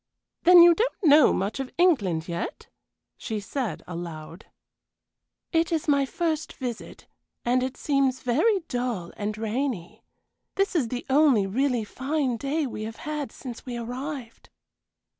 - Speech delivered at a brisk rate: No, average, 140 wpm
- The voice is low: No, very high, 255 Hz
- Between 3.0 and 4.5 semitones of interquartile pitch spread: No, average, 5.3 semitones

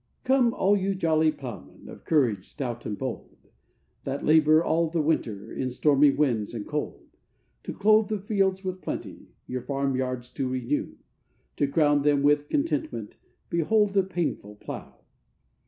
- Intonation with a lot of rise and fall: Yes, wide, 6.4 semitones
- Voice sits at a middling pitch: Yes, medium, 150 Hz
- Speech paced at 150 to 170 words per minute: Yes, average, 155 wpm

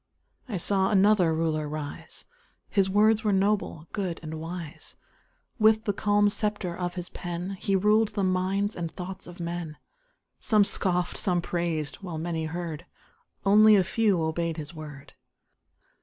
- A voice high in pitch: No, medium, 180 Hz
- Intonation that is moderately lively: Yes, average, 3.6 semitones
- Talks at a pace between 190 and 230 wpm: No, average, 150 wpm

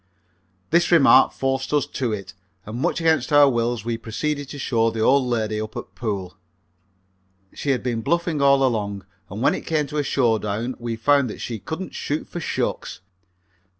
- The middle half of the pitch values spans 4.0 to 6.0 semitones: Yes, average, 4.4 semitones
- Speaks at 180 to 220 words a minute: Yes, average, 185 wpm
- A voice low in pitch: Yes, low, 125 Hz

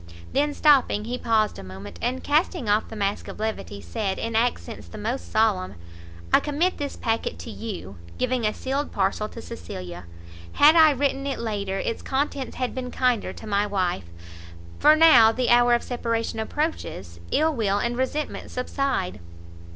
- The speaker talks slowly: No, average, 170 wpm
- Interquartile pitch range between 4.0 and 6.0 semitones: Yes, average, 4.7 semitones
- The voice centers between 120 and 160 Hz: No, high, 230 Hz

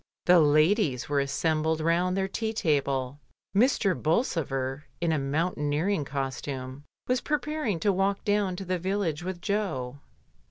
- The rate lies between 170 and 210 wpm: No, average, 145 wpm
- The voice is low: No, medium, 165 Hz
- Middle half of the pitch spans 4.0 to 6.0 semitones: Yes, wide, 5.6 semitones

